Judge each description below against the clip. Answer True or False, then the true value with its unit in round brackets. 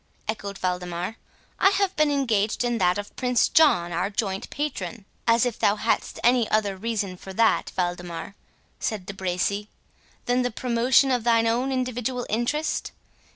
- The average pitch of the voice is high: True (225 Hz)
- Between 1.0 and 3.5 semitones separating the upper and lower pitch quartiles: False (4.3 semitones)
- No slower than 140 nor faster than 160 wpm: True (155 wpm)